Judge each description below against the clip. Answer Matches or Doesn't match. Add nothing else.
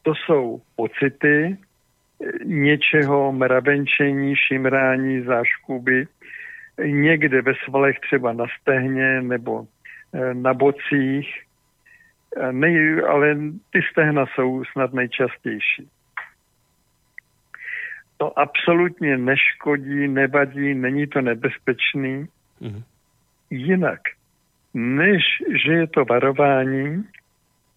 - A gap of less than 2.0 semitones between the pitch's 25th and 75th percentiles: Doesn't match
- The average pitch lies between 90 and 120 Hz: Doesn't match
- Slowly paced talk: Matches